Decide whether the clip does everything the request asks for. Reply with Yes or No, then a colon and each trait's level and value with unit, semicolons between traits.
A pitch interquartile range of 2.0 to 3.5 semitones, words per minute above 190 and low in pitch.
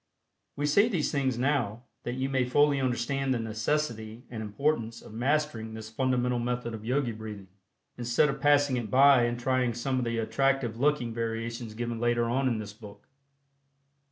No: average, 3.1 semitones; average, 175 wpm; low, 120 Hz